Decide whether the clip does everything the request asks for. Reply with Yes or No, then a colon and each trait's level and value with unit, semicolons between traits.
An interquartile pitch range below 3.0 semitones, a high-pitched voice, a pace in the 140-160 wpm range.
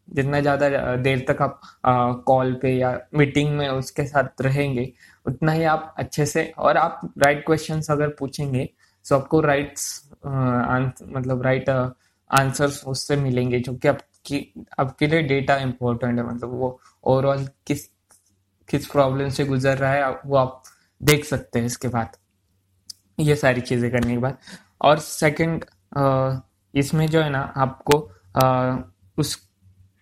No: narrow, 2.5 semitones; low, 135 Hz; average, 155 wpm